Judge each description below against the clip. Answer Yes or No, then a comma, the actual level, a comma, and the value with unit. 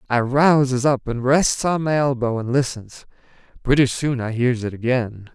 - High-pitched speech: No, low, 130 Hz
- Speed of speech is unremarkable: Yes, average, 180 wpm